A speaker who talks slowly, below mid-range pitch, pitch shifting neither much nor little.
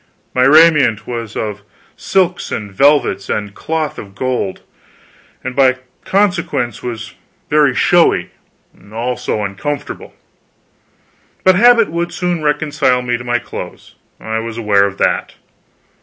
No: slow, 125 wpm; low, 125 Hz; wide, 6.2 semitones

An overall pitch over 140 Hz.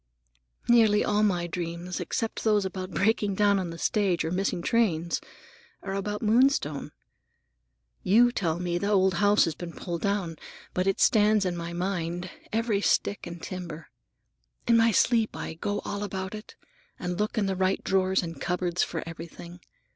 Yes: high, 190 Hz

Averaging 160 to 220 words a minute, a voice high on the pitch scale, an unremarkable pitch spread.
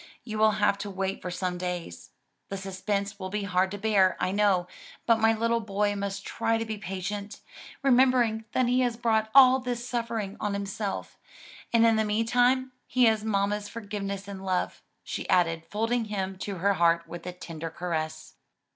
Yes: average, 180 wpm; high, 205 Hz; average, 3.0 semitones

